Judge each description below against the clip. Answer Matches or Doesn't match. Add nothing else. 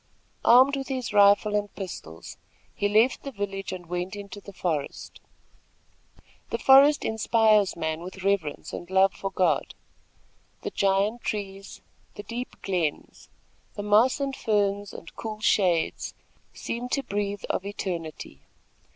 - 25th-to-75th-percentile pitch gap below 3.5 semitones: Matches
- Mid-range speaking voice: Doesn't match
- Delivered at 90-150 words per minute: Matches